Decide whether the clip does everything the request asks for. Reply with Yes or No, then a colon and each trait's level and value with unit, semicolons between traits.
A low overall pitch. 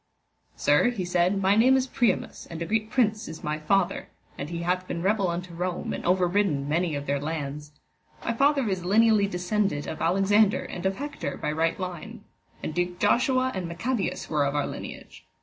No: medium, 180 Hz